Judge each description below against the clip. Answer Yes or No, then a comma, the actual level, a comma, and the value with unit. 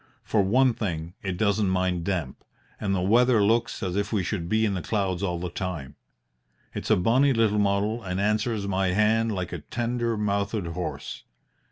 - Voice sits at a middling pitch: No, low, 100 Hz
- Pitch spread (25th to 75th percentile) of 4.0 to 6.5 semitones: No, average, 3.3 semitones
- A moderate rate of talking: Yes, average, 185 wpm